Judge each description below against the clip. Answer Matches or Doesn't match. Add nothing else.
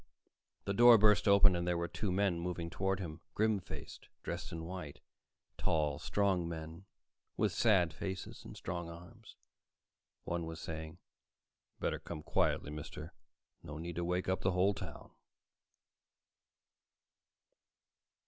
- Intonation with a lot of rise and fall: Doesn't match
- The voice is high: Doesn't match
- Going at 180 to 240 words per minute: Doesn't match